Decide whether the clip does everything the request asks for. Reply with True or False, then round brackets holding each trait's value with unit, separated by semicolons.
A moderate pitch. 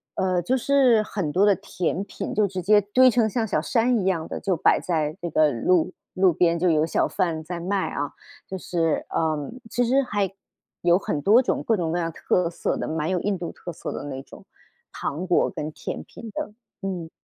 True (180 Hz)